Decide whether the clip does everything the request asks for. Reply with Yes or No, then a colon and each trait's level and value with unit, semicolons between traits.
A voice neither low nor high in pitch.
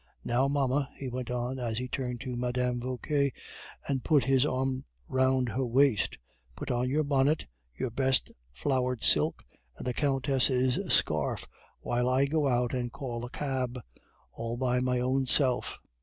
No: low, 130 Hz